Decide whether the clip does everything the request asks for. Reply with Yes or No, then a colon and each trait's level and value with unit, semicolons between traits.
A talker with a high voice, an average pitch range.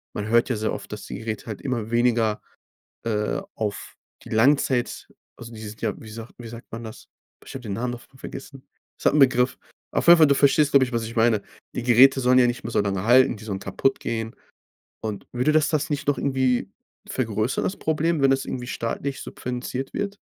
No: low, 120 Hz; average, 3.2 semitones